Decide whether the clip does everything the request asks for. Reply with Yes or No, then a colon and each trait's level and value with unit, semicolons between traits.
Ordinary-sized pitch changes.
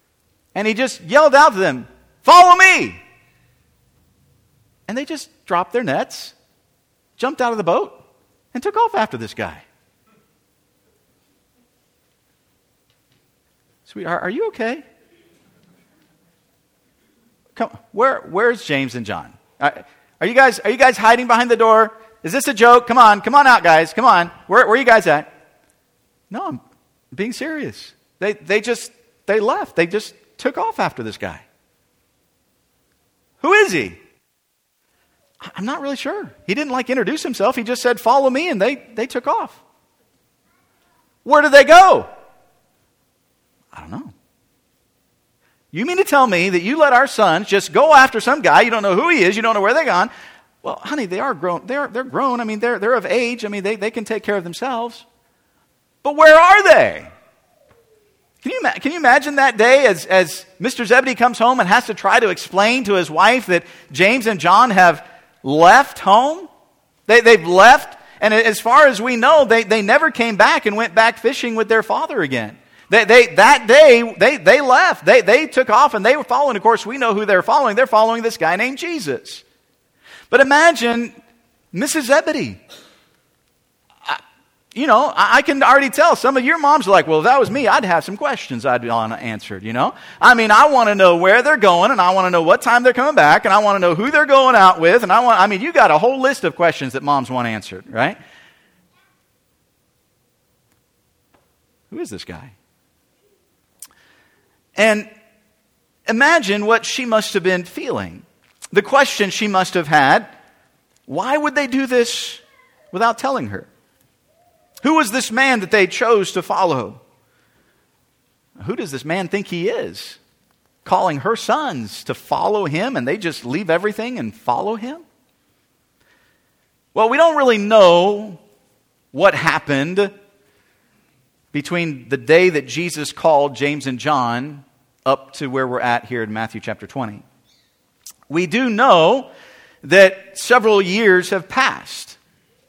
No: wide, 6.4 semitones